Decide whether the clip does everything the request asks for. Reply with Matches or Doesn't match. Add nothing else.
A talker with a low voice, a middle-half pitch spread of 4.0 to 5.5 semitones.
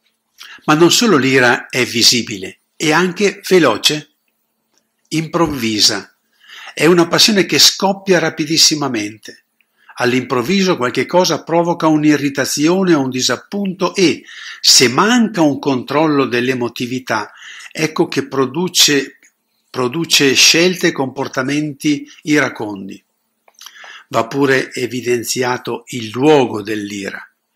Doesn't match